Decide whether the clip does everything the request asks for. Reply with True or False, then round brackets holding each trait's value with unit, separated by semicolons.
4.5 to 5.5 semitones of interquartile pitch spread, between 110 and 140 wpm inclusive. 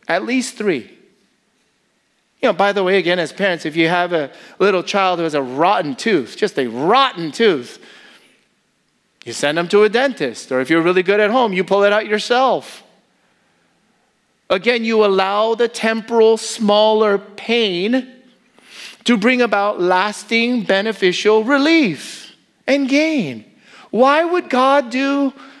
False (4.9 semitones; 150 wpm)